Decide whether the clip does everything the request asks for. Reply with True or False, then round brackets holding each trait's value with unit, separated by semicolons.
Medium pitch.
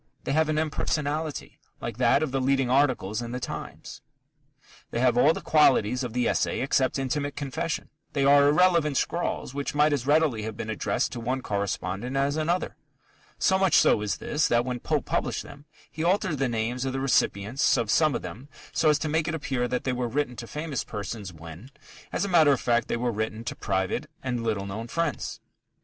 False (130 Hz)